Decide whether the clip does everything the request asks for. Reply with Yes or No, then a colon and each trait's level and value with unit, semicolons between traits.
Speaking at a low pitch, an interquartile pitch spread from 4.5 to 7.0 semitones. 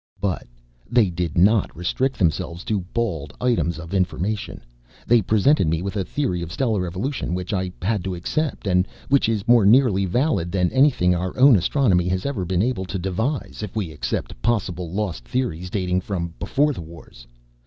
Yes: very low, 95 Hz; average, 4.8 semitones